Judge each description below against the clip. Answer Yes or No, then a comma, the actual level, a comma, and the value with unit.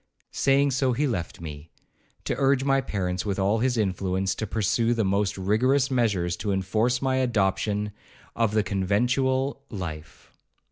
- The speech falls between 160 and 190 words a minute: No, average, 150 wpm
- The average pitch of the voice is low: Yes, low, 110 Hz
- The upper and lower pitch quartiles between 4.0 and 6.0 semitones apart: Yes, average, 5.1 semitones